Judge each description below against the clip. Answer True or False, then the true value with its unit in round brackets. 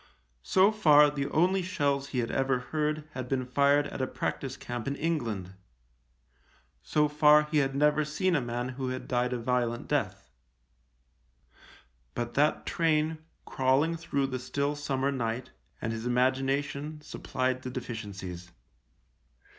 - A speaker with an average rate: True (145 wpm)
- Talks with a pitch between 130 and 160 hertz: True (135 Hz)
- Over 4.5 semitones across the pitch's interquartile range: False (3.2 semitones)